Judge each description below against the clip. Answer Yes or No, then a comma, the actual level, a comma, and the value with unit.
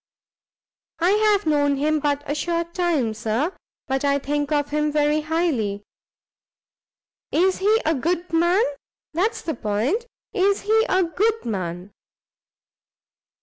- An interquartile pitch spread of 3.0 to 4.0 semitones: No, average, 4.5 semitones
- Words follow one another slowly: Yes, slow, 130 wpm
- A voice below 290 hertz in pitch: No, very high, 310 Hz